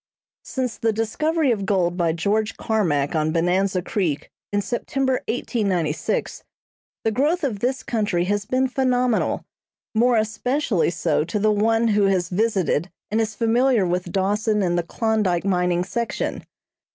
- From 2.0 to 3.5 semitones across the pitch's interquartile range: No, average, 4.7 semitones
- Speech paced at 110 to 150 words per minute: Yes, average, 145 wpm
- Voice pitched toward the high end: Yes, high, 210 Hz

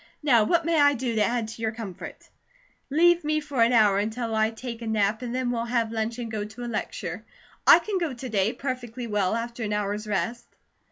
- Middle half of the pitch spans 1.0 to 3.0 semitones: Yes, average, 2.7 semitones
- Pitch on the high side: Yes, high, 230 Hz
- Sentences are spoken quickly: Yes, fast, 225 wpm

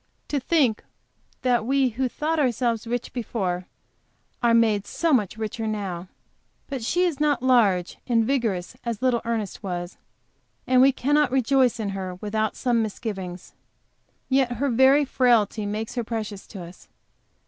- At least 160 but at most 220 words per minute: No, average, 150 wpm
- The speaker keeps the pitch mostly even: No, average, 3.9 semitones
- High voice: Yes, high, 230 Hz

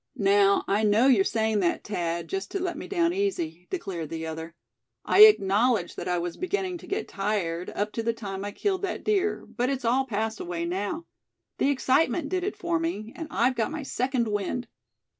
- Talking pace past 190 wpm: Yes, average, 200 wpm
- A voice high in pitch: Yes, high, 230 Hz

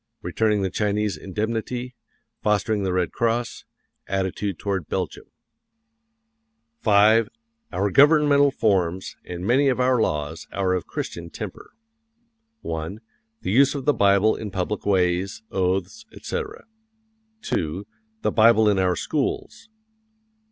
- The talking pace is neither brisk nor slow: No, slow, 125 wpm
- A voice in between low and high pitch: No, low, 105 Hz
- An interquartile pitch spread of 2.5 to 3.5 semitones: No, average, 4.5 semitones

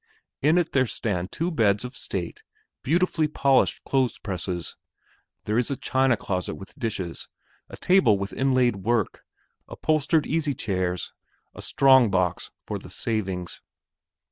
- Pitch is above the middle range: No, low, 120 Hz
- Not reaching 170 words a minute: Yes, average, 140 wpm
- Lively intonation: Yes, wide, 6.2 semitones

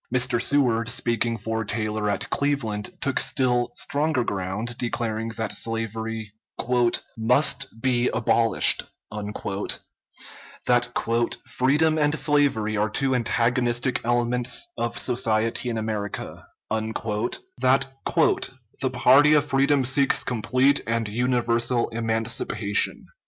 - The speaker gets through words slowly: Yes, slow, 100 wpm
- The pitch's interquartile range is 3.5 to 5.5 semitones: No, narrow, 2.6 semitones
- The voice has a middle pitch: No, low, 120 Hz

